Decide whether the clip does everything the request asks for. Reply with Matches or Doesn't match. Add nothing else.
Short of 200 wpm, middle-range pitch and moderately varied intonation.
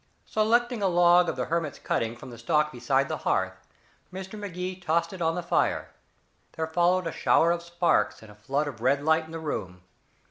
Doesn't match